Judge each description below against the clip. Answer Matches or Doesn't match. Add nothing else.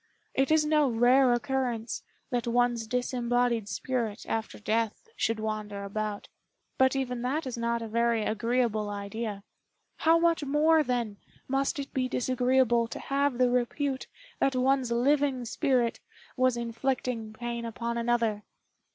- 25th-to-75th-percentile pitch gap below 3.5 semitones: Matches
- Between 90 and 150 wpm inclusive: Matches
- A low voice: Doesn't match